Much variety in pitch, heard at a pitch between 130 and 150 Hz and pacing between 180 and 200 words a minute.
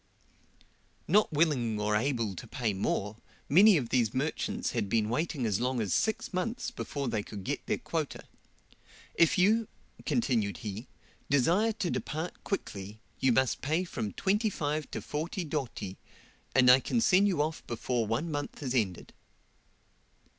No: wide, 7.6 semitones; low, 135 Hz; average, 155 wpm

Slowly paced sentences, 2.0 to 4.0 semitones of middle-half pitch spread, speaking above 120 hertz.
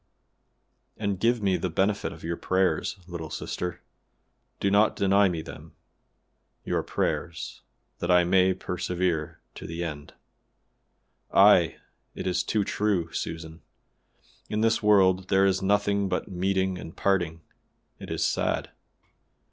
No: slow, 130 wpm; average, 2.7 semitones; very low, 95 Hz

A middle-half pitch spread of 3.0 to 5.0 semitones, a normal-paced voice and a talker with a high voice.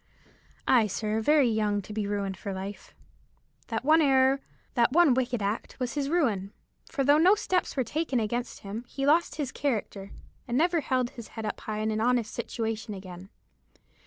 Yes: average, 4.7 semitones; average, 180 wpm; high, 240 Hz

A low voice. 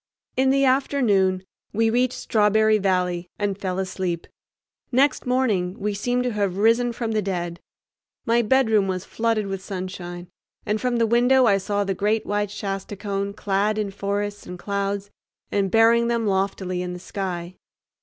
No: high, 205 Hz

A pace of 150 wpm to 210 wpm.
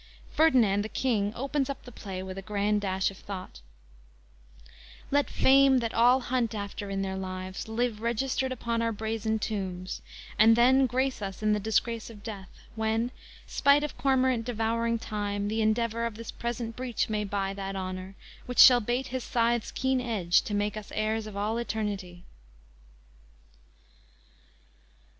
Yes: average, 160 wpm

